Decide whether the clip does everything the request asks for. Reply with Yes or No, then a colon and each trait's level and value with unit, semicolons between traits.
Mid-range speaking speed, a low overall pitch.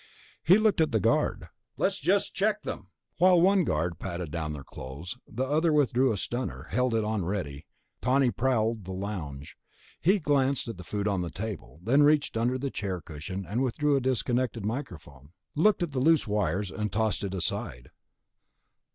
Yes: average, 180 wpm; low, 110 Hz